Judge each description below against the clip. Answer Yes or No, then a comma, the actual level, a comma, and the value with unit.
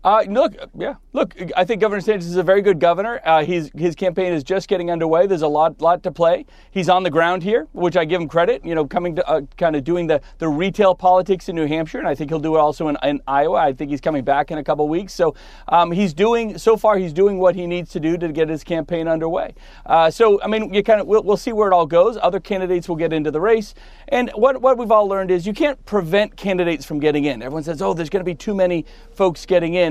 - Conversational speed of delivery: No, fast, 270 wpm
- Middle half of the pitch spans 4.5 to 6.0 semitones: No, average, 3.7 semitones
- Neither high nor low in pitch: Yes, medium, 180 Hz